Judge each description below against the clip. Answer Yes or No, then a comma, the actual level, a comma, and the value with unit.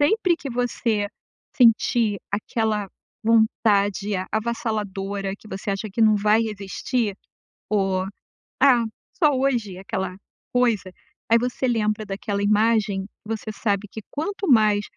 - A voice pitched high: Yes, high, 215 Hz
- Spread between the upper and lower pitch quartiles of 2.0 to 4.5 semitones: Yes, narrow, 2.6 semitones